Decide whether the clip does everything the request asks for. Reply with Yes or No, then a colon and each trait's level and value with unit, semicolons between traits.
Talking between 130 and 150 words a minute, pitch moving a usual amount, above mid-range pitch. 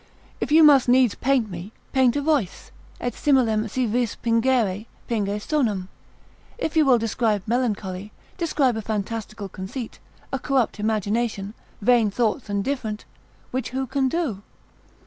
Yes: average, 145 wpm; average, 4.0 semitones; high, 230 Hz